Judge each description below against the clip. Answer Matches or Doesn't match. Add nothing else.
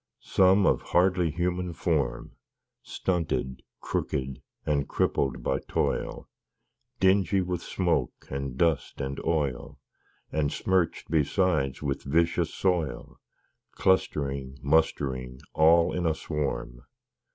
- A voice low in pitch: Matches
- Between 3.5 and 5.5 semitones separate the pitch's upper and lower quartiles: Matches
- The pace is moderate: Doesn't match